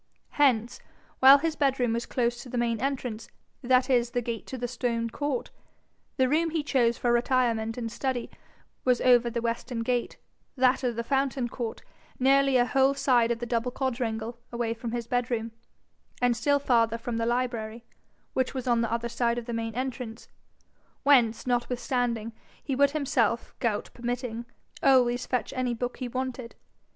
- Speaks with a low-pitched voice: No, high, 245 Hz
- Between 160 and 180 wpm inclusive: Yes, average, 170 wpm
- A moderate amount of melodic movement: No, narrow, 1.8 semitones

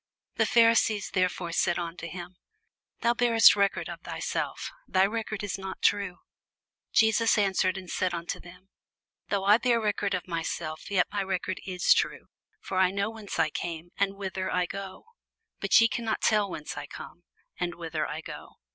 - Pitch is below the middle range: No, high, 190 Hz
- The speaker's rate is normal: Yes, average, 175 wpm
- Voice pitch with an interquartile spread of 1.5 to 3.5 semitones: Yes, average, 2.8 semitones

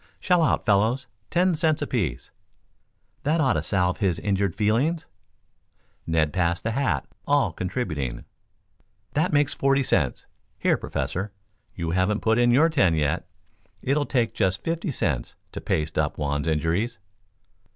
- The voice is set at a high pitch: No, low, 105 Hz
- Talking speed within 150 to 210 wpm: No, average, 140 wpm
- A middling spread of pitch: No, wide, 8.9 semitones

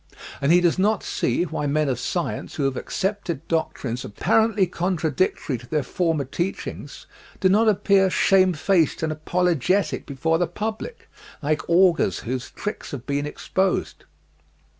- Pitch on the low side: No, medium, 170 Hz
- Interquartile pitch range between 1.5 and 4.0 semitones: No, average, 4.8 semitones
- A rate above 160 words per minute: No, average, 140 wpm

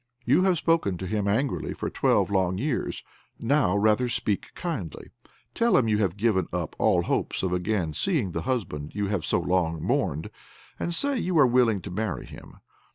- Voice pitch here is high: No, low, 105 Hz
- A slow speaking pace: No, average, 185 wpm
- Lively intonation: Yes, wide, 6.4 semitones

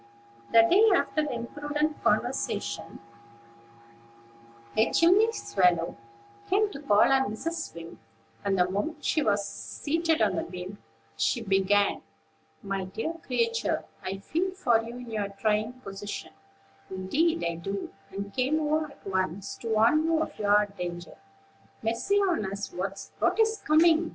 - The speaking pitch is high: Yes, high, 225 Hz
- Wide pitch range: Yes, wide, 8.2 semitones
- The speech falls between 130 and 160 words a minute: Yes, average, 140 wpm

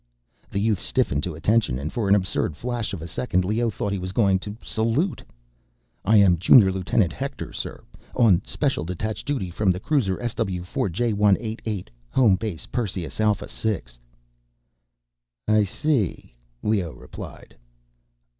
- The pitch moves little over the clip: No, average, 3.6 semitones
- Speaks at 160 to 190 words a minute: No, average, 145 wpm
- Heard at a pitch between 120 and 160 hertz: No, low, 100 Hz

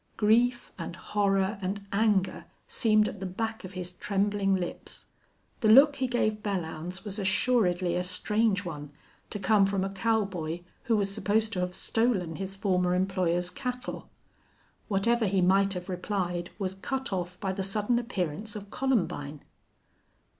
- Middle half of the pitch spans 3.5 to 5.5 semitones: No, average, 3.0 semitones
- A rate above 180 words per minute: No, average, 155 wpm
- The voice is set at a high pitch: Yes, high, 195 Hz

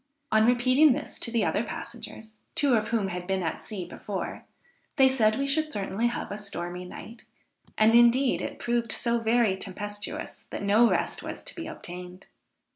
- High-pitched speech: Yes, high, 220 Hz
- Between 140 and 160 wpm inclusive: No, average, 180 wpm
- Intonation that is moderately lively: Yes, average, 3.2 semitones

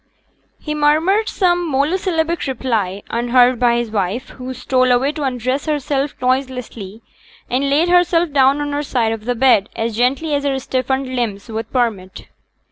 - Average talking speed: Yes, average, 160 wpm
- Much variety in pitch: No, average, 3.6 semitones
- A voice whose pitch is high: Yes, very high, 260 Hz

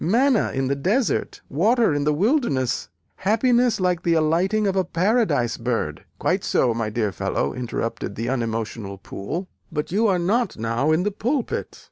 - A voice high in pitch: No, medium, 165 Hz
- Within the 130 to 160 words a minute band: No, average, 170 wpm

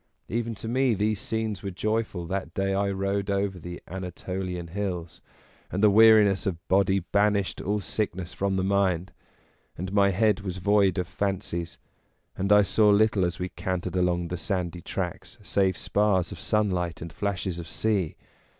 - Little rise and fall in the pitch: Yes, narrow, 2.3 semitones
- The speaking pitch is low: Yes, very low, 95 Hz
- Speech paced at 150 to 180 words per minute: Yes, average, 170 wpm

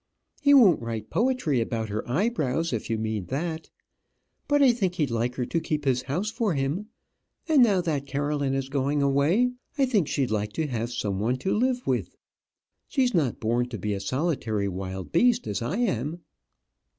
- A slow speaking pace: No, average, 185 wpm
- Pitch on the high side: No, medium, 140 Hz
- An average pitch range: No, wide, 8.4 semitones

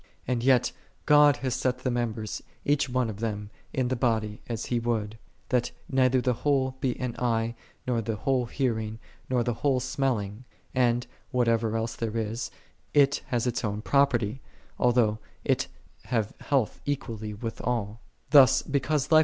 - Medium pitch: No, low, 120 Hz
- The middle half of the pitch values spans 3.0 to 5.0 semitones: No, narrow, 2.4 semitones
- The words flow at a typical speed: Yes, average, 160 wpm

